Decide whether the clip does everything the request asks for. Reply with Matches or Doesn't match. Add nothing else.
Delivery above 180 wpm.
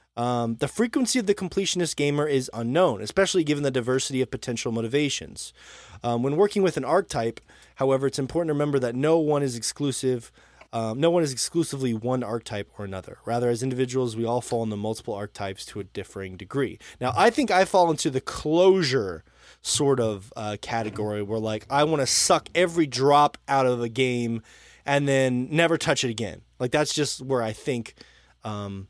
Matches